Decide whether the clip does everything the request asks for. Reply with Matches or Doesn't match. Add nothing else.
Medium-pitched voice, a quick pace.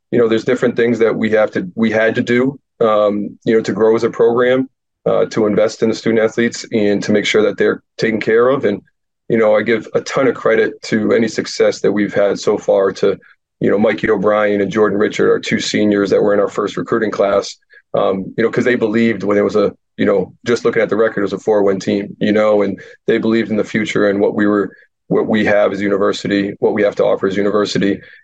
Doesn't match